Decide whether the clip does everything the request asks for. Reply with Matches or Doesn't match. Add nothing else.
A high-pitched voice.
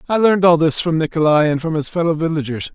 Doesn't match